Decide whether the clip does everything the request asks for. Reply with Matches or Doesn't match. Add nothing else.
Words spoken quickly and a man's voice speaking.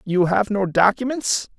Doesn't match